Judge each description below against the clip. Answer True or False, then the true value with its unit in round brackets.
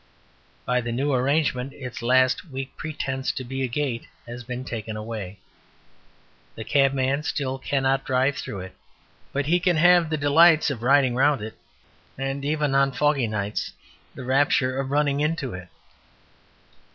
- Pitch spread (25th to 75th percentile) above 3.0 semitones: False (2.6 semitones)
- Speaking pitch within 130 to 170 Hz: True (135 Hz)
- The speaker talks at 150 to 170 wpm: True (155 wpm)